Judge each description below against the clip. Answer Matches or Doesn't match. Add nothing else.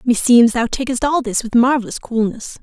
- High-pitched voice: Matches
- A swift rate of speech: Doesn't match